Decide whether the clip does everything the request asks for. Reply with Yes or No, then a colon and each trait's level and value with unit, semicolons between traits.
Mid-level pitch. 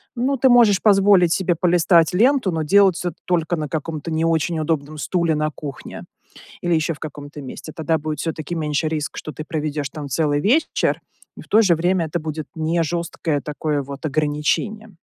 Yes: medium, 160 Hz